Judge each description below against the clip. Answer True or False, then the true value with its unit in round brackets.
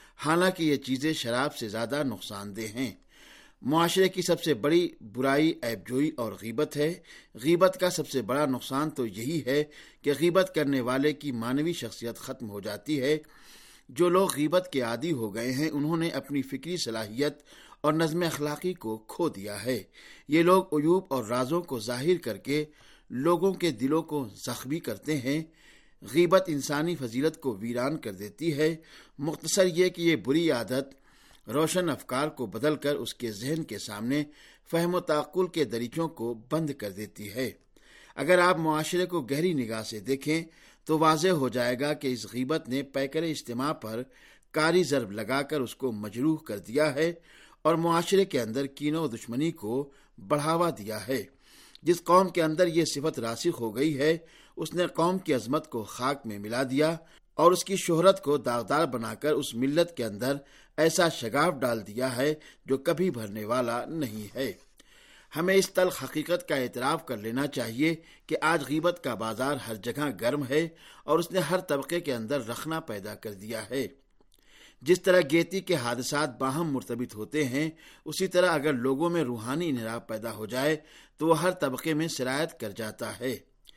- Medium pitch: True (150 Hz)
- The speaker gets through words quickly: False (180 wpm)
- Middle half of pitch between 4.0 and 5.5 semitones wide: True (4.9 semitones)